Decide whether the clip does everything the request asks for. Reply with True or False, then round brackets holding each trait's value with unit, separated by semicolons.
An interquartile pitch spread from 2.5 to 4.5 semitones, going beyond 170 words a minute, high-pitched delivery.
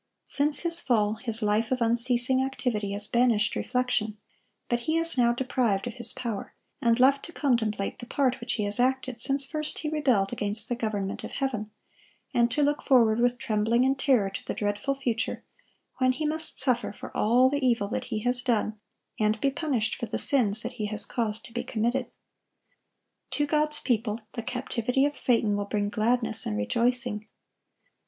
True (3.5 semitones; 185 wpm; 240 Hz)